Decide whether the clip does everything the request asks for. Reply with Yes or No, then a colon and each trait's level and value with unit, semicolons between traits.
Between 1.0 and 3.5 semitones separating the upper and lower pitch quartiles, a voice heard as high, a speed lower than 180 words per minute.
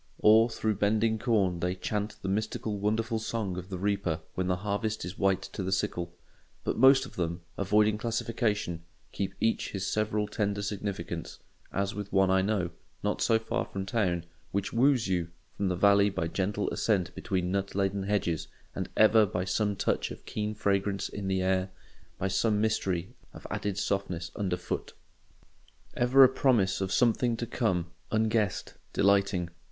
No: narrow, 2.6 semitones; low, 100 Hz; average, 170 wpm